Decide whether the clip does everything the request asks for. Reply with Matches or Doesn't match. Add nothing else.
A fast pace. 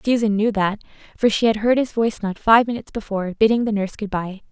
Matches